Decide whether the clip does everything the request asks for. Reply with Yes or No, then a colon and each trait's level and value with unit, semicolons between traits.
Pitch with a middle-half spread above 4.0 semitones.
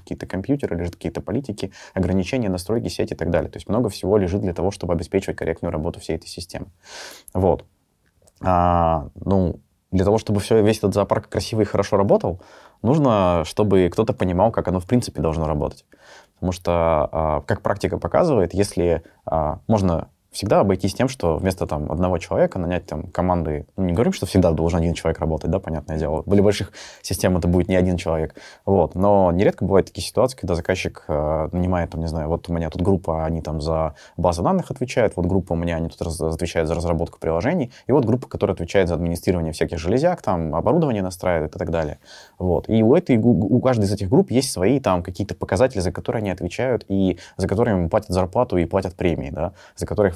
No: average, 3.3 semitones